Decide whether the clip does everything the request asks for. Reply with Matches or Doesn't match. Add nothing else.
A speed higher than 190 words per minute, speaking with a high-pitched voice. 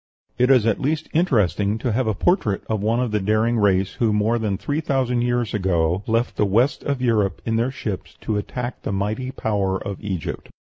Doesn't match